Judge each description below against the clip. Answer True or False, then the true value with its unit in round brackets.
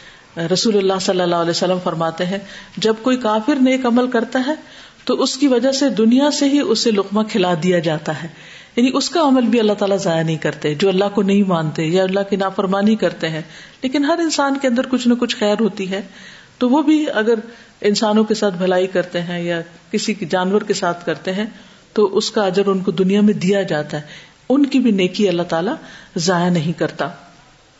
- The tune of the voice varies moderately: True (4.7 semitones)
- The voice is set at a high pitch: True (200 Hz)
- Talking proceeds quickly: True (210 wpm)